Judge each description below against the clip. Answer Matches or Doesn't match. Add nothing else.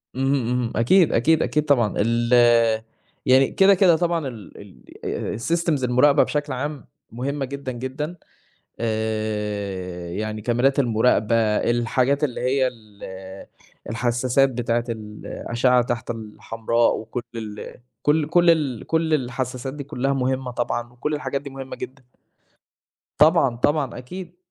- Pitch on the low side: Matches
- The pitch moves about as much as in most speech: Matches